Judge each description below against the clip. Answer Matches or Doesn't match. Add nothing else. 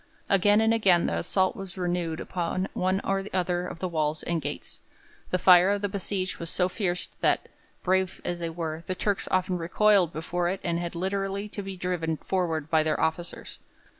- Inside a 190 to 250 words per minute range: Matches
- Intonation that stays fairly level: Matches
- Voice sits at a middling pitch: Matches